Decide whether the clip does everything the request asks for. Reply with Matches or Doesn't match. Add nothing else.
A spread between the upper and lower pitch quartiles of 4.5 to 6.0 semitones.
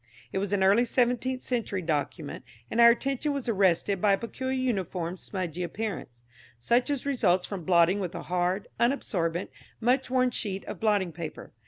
Matches